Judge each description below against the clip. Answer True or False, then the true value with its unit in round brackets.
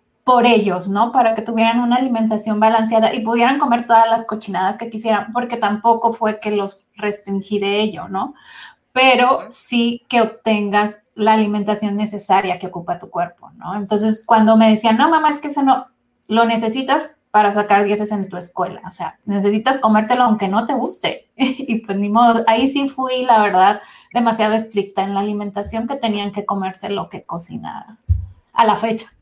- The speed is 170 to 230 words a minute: True (180 wpm)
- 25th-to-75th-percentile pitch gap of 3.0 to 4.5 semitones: False (2.4 semitones)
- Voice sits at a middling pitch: False (220 Hz)